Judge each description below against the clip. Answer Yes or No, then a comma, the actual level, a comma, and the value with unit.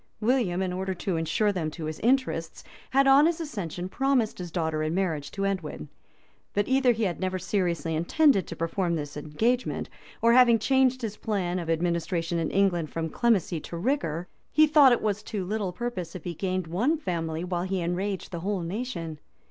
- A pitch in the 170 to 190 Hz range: Yes, medium, 185 Hz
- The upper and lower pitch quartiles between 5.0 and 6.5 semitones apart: Yes, wide, 5.5 semitones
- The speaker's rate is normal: Yes, average, 190 wpm